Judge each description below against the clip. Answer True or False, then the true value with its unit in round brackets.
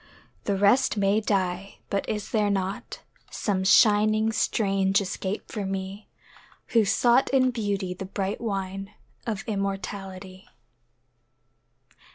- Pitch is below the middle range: False (200 Hz)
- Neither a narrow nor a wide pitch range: False (1.8 semitones)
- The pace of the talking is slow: True (115 wpm)